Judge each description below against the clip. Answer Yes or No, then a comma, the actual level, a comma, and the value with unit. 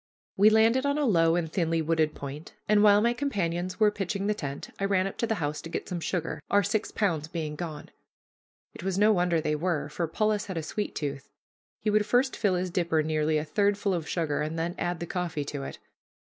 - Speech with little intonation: No, average, 4.5 semitones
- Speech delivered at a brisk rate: Yes, fast, 230 wpm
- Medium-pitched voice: Yes, medium, 175 Hz